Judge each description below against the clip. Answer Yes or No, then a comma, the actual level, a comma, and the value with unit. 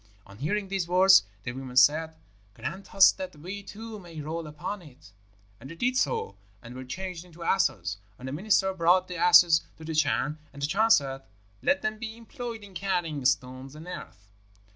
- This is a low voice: No, medium, 170 Hz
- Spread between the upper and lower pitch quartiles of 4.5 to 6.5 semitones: Yes, wide, 5.4 semitones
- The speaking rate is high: No, average, 190 wpm